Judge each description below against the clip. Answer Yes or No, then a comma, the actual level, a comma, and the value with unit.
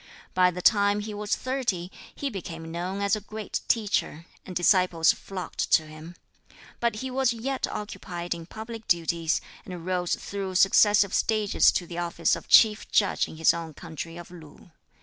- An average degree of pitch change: Yes, average, 3.7 semitones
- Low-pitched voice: No, medium, 185 Hz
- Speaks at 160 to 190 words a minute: Yes, average, 170 wpm